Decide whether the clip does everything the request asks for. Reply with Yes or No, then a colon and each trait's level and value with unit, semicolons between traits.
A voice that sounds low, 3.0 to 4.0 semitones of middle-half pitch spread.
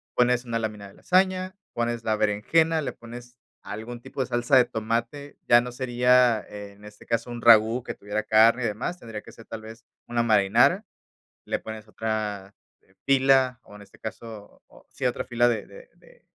No: low, 115 Hz; narrow, 2.5 semitones